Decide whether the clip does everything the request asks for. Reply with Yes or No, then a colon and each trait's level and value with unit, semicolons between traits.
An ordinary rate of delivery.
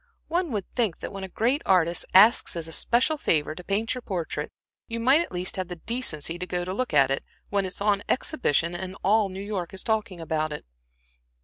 No: fast, 225 wpm